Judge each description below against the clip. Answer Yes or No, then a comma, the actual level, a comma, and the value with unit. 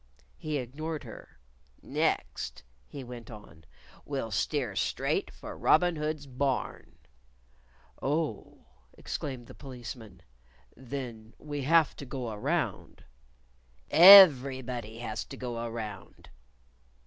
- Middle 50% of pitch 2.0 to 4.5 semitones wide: Yes, average, 4.1 semitones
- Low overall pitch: Yes, low, 130 Hz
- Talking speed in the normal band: No, slow, 100 wpm